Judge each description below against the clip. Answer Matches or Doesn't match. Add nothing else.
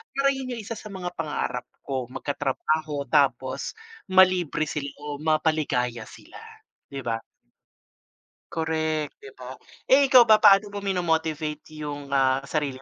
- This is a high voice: Doesn't match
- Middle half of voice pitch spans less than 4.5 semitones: Doesn't match